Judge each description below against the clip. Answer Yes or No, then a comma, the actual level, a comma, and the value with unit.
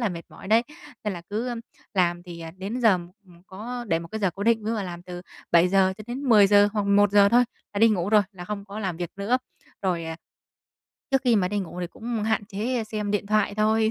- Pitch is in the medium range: No, high, 205 Hz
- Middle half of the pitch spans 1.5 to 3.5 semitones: Yes, average, 3.2 semitones